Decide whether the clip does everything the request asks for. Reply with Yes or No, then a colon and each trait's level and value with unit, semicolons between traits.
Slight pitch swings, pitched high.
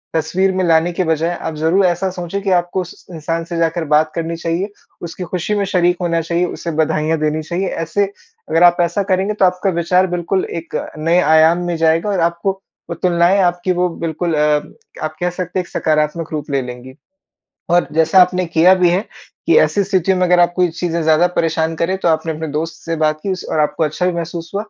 No: narrow, 2.1 semitones; medium, 170 Hz